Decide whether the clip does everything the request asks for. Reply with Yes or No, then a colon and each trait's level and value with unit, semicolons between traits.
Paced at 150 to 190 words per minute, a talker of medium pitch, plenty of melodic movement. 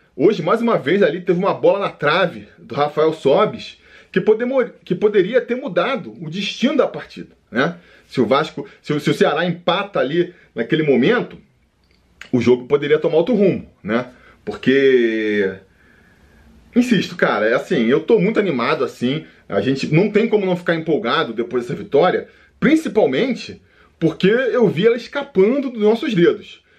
Yes: average, 165 wpm; medium, 180 Hz; wide, 7.4 semitones